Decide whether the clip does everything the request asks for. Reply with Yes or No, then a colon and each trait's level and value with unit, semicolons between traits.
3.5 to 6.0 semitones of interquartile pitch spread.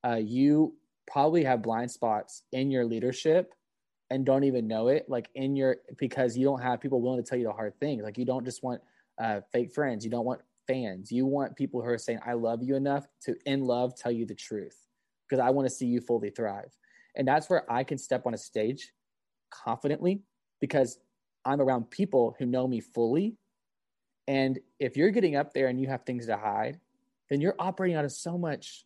No: narrow, 2.6 semitones